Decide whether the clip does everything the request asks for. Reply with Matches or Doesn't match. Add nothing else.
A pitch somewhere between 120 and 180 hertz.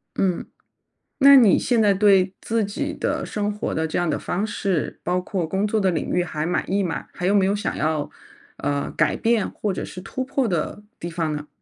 Doesn't match